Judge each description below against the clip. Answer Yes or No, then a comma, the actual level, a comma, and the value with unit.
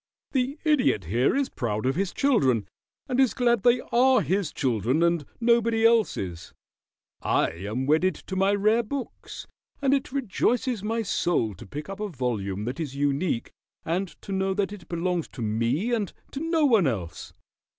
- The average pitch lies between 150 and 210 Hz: Yes, high, 190 Hz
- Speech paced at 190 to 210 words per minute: No, average, 170 wpm